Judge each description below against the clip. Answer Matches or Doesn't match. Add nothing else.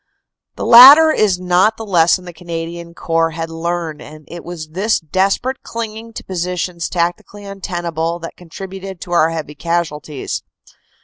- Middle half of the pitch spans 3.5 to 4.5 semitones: Doesn't match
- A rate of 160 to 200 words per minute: Doesn't match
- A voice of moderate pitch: Matches